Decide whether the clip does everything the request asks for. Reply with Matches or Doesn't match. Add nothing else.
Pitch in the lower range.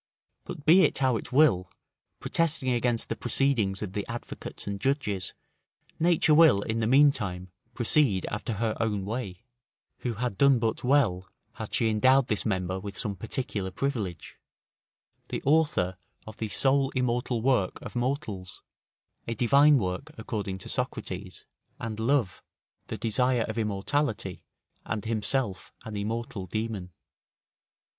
Matches